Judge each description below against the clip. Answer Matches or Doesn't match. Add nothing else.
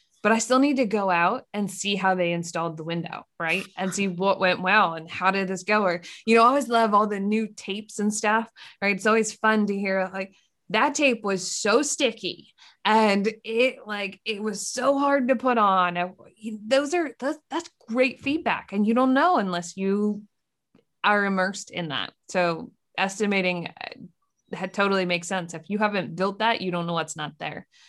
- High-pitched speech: Matches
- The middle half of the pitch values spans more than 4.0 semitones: Doesn't match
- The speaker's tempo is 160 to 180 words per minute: Doesn't match